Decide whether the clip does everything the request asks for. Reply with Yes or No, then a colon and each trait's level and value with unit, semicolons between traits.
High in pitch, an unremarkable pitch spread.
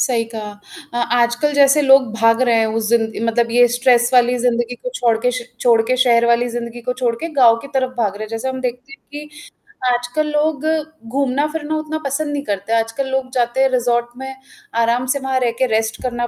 No: high, 245 Hz; narrow, 2.3 semitones